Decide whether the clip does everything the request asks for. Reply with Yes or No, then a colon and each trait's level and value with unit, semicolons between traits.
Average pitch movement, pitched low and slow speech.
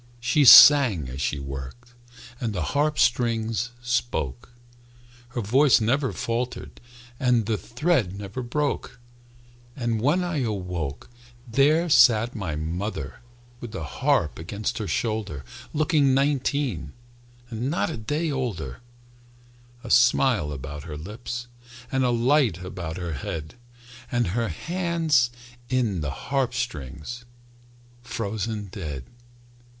No: wide, 6.7 semitones; low, 115 Hz; slow, 120 wpm